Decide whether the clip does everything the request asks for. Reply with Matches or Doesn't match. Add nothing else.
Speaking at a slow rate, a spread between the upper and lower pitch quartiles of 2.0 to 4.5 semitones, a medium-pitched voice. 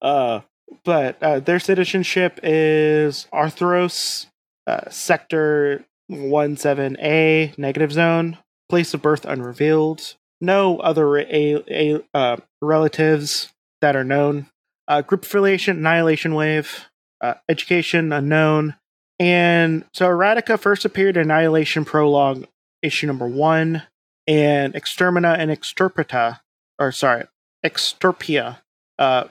Matches